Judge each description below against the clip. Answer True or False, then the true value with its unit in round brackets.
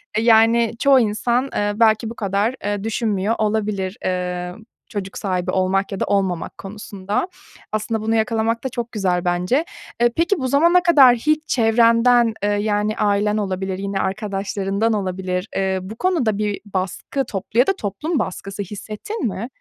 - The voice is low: False (210 Hz)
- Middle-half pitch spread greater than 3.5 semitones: False (3.1 semitones)